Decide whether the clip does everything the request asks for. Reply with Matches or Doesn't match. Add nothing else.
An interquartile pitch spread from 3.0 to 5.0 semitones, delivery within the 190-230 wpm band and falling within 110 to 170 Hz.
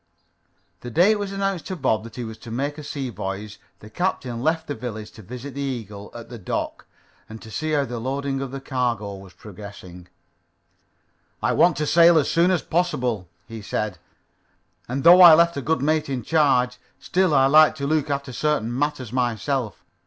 Doesn't match